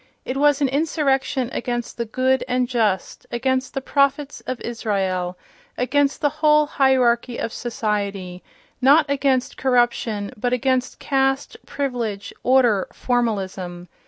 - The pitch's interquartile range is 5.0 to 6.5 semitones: No, average, 3.4 semitones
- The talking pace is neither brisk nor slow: No, slow, 120 wpm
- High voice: Yes, very high, 250 Hz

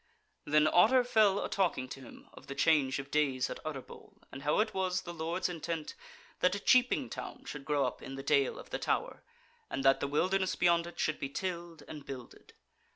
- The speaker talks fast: Yes, fast, 215 wpm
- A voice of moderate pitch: Yes, medium, 155 Hz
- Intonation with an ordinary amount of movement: Yes, average, 4.8 semitones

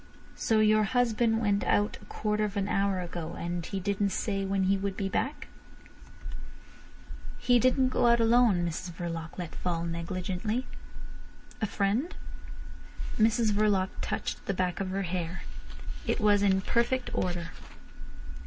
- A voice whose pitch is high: Yes, high, 200 Hz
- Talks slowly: No, average, 145 wpm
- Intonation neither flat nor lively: Yes, average, 3.4 semitones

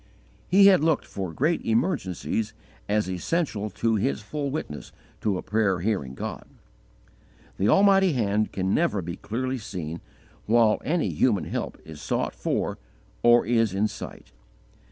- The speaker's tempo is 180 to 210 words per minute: No, average, 145 wpm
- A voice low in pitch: Yes, low, 110 Hz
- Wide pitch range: Yes, wide, 6.1 semitones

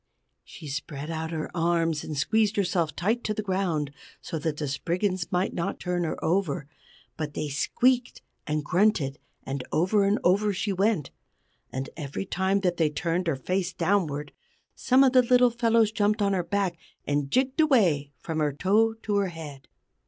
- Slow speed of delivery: No, average, 175 wpm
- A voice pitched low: No, medium, 180 Hz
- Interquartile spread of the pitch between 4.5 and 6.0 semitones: Yes, average, 5.2 semitones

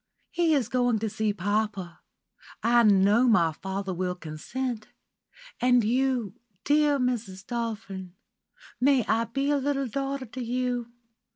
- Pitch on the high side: Yes, high, 230 Hz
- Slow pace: Yes, slow, 130 wpm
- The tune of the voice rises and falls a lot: No, average, 4.2 semitones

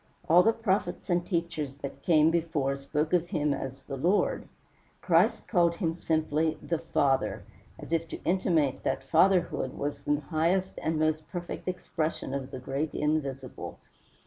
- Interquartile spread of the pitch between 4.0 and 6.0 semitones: No, average, 3.4 semitones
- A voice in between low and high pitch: Yes, medium, 155 Hz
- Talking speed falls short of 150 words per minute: No, average, 155 wpm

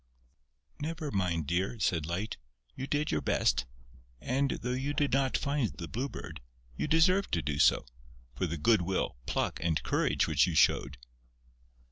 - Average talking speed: Yes, average, 165 wpm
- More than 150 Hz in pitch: No, low, 100 Hz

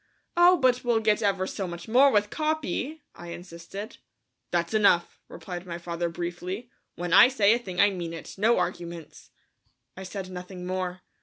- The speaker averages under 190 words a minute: Yes, average, 170 wpm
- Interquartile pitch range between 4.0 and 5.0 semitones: Yes, average, 4.3 semitones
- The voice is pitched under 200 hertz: Yes, medium, 185 Hz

